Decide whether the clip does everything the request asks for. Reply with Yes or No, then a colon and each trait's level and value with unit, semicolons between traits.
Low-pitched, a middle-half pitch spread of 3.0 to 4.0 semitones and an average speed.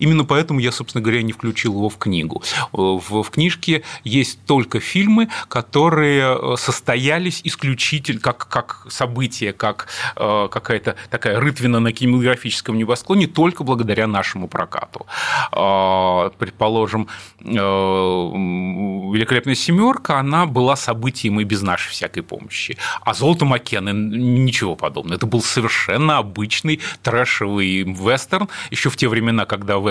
No: low, 120 Hz; average, 5.2 semitones; average, 130 wpm